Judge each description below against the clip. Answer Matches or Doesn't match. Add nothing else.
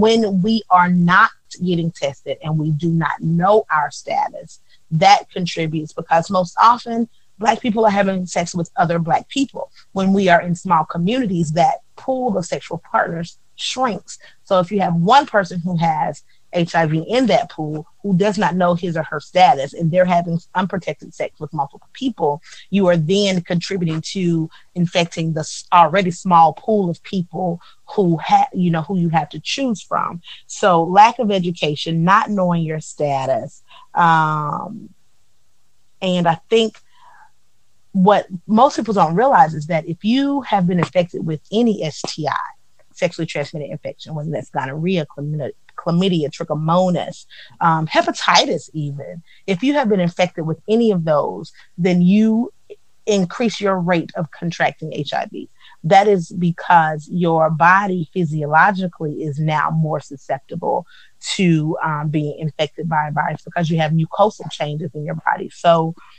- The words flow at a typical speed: Matches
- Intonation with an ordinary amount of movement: Matches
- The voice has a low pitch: Doesn't match